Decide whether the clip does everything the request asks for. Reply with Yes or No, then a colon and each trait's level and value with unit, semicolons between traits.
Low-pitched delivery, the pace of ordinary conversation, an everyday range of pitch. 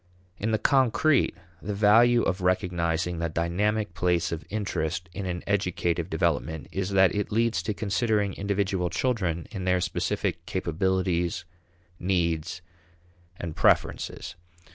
No: very low, 95 Hz; slow, 125 wpm; average, 3.2 semitones